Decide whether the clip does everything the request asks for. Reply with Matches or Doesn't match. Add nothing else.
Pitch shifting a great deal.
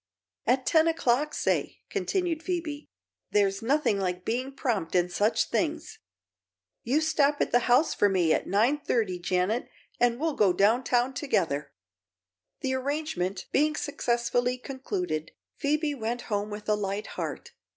Matches